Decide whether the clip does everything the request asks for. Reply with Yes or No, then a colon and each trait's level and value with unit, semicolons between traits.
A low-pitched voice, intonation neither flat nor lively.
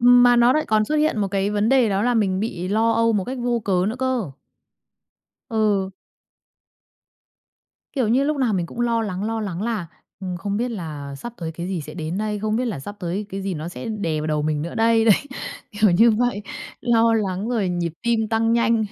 No: high, 215 Hz; average, 4.0 semitones